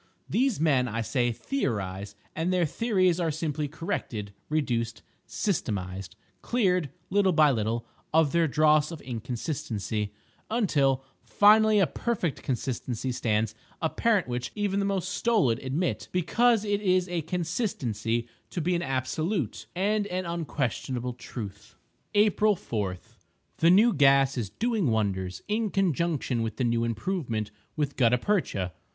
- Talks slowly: Yes, slow, 130 wpm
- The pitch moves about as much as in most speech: No, wide, 8.0 semitones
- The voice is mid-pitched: Yes, medium, 150 Hz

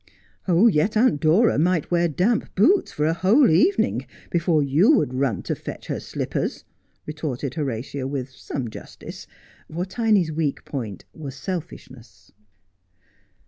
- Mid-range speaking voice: Yes, medium, 155 Hz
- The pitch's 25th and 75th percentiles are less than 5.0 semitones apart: No, wide, 5.4 semitones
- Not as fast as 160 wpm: Yes, average, 140 wpm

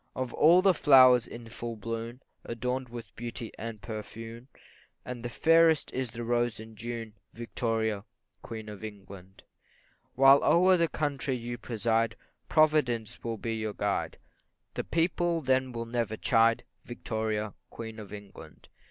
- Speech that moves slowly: No, average, 145 wpm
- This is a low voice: Yes, low, 115 Hz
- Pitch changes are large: No, average, 2.7 semitones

